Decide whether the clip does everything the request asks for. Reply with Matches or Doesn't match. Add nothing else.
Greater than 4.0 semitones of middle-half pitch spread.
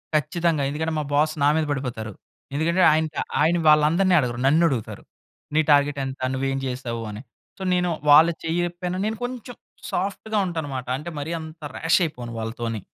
Matches